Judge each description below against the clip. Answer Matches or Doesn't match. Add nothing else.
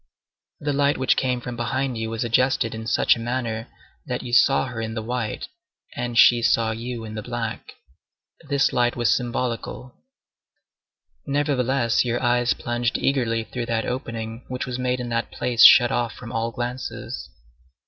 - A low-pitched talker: Matches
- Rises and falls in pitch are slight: Matches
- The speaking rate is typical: Matches